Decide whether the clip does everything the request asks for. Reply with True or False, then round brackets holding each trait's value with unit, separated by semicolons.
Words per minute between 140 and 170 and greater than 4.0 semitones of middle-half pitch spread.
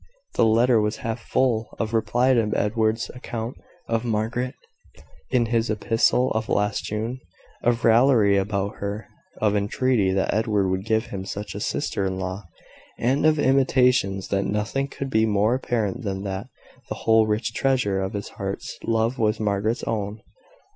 False (160 wpm; 2.8 semitones)